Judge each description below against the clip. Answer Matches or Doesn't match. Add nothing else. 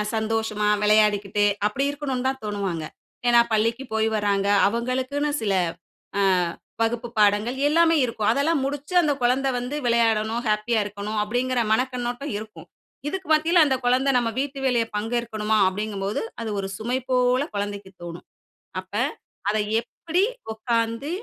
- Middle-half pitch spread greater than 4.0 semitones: Doesn't match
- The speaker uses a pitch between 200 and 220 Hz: Doesn't match